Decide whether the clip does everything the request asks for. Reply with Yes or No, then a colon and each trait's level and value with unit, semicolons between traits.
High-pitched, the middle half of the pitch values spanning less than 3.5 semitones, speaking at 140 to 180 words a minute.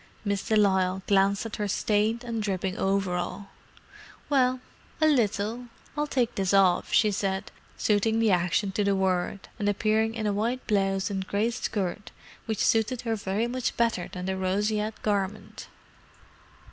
Yes: high, 205 Hz; average, 2.7 semitones; average, 160 wpm